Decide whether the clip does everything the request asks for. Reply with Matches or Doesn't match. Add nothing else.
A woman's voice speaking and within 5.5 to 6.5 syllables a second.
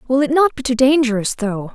Matches